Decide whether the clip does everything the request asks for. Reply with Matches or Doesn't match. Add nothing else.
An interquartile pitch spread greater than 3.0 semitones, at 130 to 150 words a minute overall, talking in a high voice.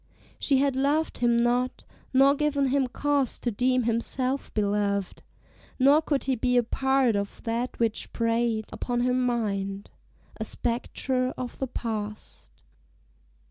Doesn't match